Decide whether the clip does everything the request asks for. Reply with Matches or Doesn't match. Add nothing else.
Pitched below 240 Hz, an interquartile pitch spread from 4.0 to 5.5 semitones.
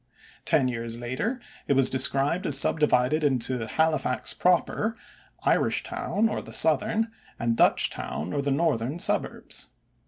Matches